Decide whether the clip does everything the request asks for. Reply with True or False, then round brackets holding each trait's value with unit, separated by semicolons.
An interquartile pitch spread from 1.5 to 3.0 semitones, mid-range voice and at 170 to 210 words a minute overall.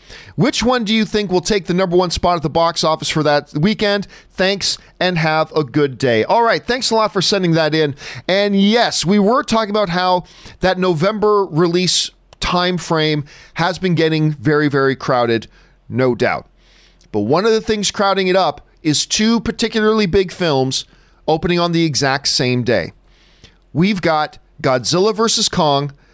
False (5.2 semitones; 175 Hz; 175 wpm)